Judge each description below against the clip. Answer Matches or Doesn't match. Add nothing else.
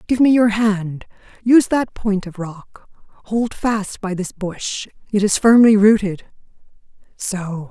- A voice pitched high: Matches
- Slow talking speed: Matches